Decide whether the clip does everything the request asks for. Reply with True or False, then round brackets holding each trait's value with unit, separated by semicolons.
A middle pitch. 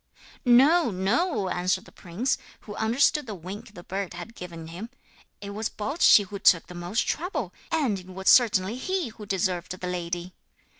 False (200 Hz)